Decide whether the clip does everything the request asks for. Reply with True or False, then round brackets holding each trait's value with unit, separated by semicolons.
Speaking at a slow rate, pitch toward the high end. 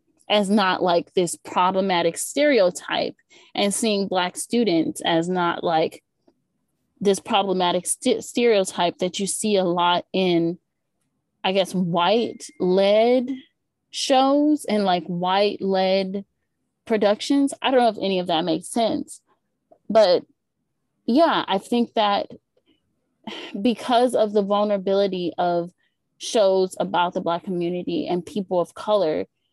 True (125 wpm; 195 Hz)